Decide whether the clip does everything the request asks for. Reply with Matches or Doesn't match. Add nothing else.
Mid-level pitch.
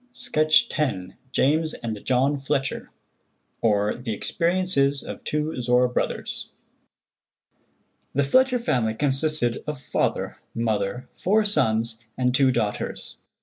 Doesn't match